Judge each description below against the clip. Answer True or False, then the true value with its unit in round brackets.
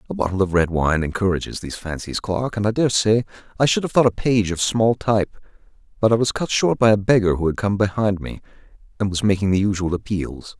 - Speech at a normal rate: False (230 wpm)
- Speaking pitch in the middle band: False (105 Hz)